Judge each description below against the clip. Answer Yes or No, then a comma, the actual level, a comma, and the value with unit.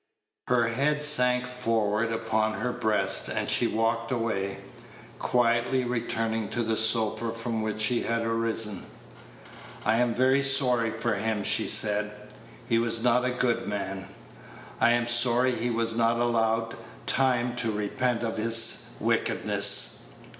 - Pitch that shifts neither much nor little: No, narrow, 1.6 semitones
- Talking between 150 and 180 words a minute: No, average, 140 wpm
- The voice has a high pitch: No, low, 115 Hz